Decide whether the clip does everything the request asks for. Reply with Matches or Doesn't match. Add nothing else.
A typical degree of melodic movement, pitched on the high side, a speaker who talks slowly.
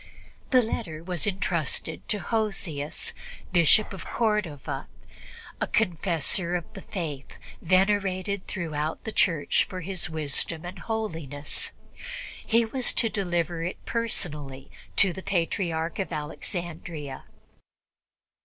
Doesn't match